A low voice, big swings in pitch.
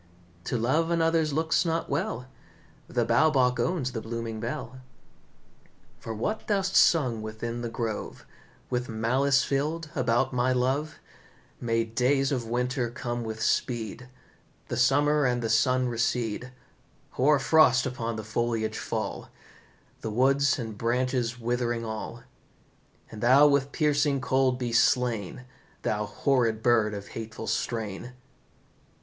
No: low, 125 Hz; average, 3.1 semitones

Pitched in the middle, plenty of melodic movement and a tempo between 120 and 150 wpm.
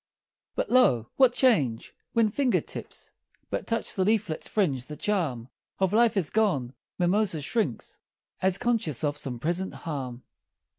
Yes: medium, 180 Hz; wide, 7.9 semitones; average, 145 wpm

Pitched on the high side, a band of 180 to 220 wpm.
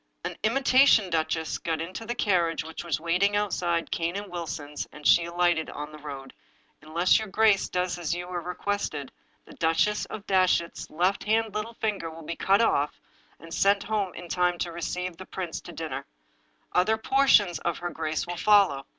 No: medium, 175 Hz; average, 190 wpm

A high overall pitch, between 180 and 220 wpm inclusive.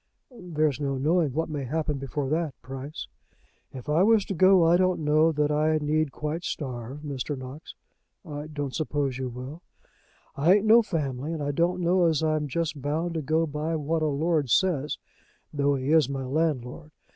No: medium, 150 Hz; average, 185 wpm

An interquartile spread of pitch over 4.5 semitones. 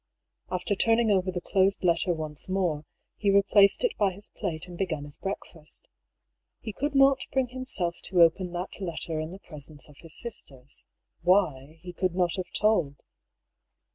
No: average, 3.8 semitones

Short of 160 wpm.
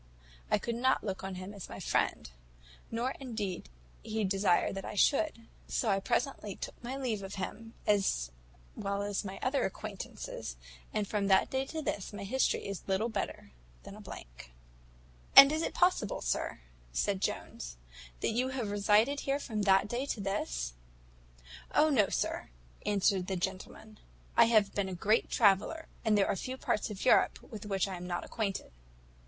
No: average, 180 wpm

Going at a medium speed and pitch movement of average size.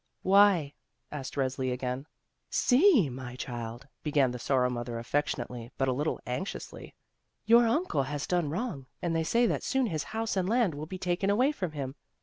No: average, 180 wpm; wide, 7.6 semitones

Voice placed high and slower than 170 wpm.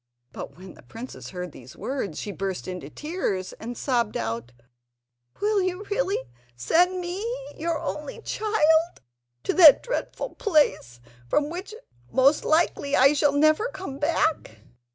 Yes: very high, 295 Hz; average, 140 wpm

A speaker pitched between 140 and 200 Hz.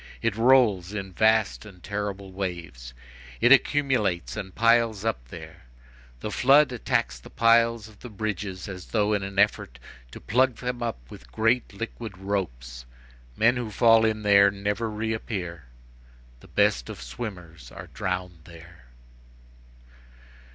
No: low, 105 Hz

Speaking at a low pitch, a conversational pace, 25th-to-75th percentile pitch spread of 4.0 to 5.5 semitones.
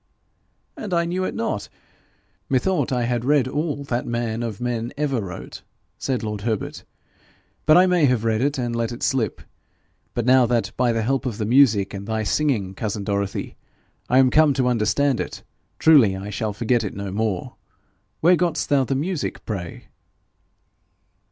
Yes: low, 120 Hz; average, 175 wpm; average, 4.5 semitones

